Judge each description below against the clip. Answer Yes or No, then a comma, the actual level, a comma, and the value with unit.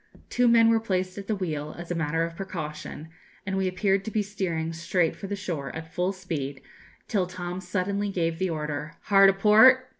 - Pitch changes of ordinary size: Yes, average, 3.6 semitones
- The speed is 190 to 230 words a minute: Yes, fast, 205 wpm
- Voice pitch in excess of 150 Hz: Yes, medium, 185 Hz